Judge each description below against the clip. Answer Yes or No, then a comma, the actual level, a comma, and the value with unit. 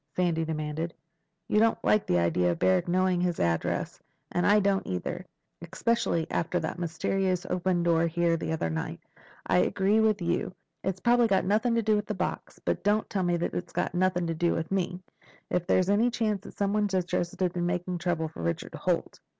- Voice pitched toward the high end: No, medium, 180 Hz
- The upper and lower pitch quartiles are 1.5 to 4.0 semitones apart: Yes, average, 3.0 semitones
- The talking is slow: No, average, 190 wpm